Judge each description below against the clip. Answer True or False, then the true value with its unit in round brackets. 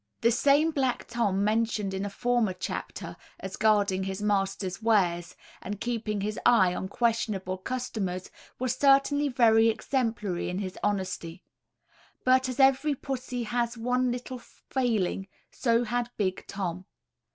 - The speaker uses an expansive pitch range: False (4.3 semitones)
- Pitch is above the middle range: True (225 Hz)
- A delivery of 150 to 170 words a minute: False (140 wpm)